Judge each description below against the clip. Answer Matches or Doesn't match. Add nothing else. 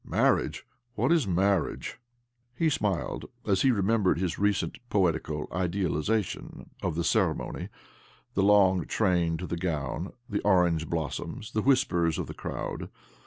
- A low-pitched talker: Matches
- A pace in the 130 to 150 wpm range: Matches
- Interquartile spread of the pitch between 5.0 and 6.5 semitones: Doesn't match